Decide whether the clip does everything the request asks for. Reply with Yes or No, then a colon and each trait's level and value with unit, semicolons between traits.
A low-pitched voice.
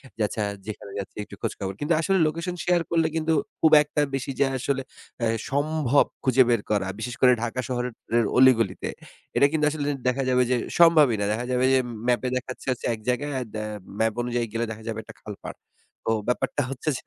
Yes: low, 125 Hz